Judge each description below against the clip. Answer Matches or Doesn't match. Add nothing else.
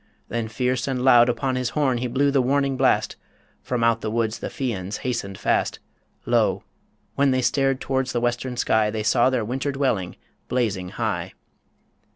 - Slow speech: Doesn't match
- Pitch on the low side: Matches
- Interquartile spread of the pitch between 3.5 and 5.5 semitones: Doesn't match